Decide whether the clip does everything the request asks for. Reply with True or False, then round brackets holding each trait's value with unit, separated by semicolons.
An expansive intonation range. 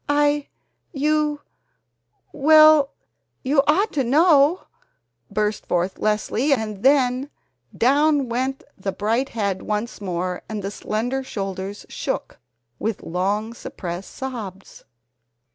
True (6.2 semitones)